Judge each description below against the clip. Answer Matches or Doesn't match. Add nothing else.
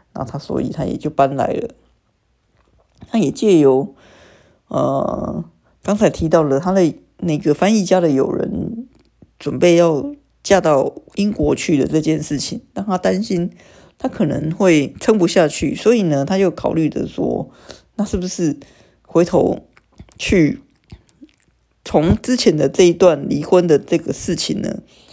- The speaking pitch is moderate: Matches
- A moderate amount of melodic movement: Matches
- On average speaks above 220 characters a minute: Doesn't match